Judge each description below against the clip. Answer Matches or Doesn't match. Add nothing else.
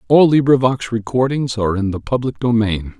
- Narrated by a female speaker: Doesn't match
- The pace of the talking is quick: Doesn't match